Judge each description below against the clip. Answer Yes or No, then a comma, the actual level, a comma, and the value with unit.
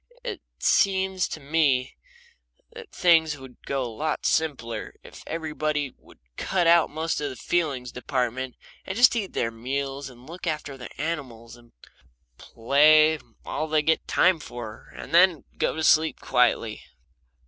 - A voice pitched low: No, medium, 150 Hz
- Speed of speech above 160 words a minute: No, average, 150 wpm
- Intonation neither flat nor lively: Yes, average, 4.3 semitones